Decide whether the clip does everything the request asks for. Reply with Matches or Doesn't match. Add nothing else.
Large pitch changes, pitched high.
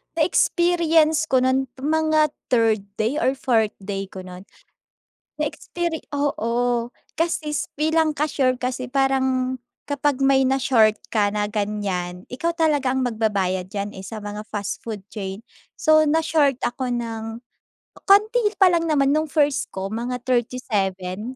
Matches